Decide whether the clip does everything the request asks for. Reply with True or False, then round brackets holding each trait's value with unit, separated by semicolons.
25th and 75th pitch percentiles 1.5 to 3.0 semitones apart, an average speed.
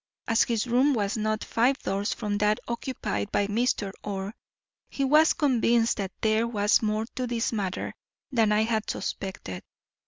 True (2.6 semitones; 160 wpm)